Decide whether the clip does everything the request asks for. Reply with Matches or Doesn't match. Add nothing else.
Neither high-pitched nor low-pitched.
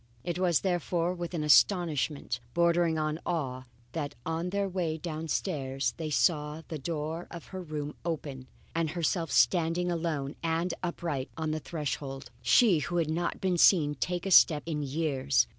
Matches